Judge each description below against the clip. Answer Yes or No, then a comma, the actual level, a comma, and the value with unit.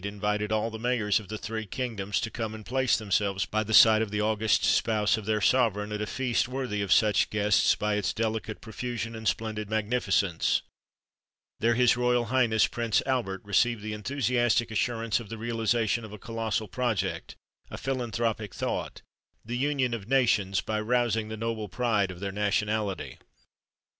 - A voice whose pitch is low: Yes, low, 110 Hz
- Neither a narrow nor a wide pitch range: No, narrow, 2.2 semitones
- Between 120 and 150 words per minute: No, average, 175 wpm